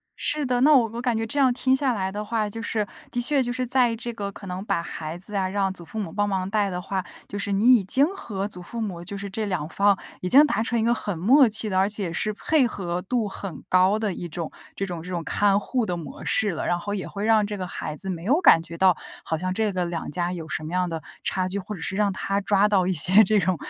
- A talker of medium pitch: No, high, 200 Hz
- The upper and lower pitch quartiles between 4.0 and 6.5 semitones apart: No, average, 3.6 semitones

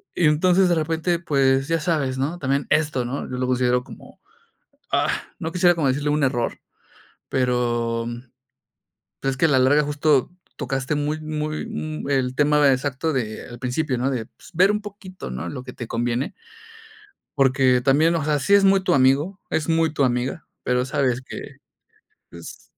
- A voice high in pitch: No, medium, 140 Hz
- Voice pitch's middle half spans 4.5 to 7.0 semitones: No, average, 3.7 semitones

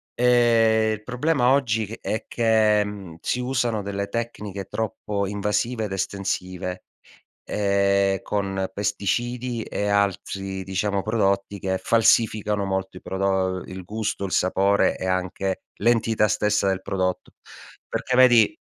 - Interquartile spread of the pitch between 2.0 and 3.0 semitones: Yes, narrow, 2.6 semitones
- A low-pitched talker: Yes, low, 100 Hz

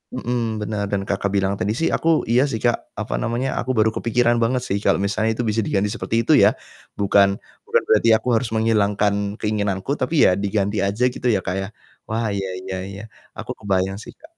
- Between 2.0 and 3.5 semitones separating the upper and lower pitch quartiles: Yes, average, 2.9 semitones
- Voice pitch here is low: Yes, low, 110 Hz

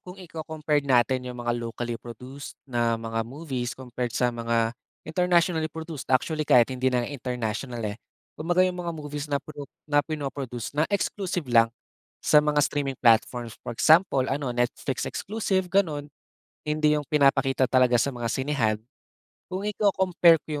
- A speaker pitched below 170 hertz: Yes, medium, 140 Hz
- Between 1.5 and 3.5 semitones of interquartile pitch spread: No, average, 4.5 semitones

